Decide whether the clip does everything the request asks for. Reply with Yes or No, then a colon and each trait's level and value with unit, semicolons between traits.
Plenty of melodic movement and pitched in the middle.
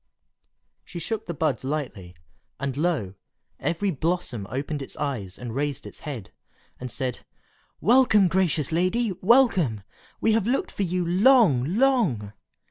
Yes: wide, 7.3 semitones; medium, 160 Hz